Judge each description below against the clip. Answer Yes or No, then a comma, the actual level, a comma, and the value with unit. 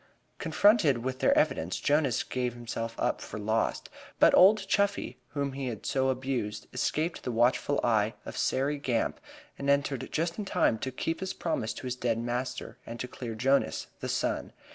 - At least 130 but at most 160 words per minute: No, average, 180 wpm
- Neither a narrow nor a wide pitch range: Yes, average, 3.6 semitones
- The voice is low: Yes, low, 130 Hz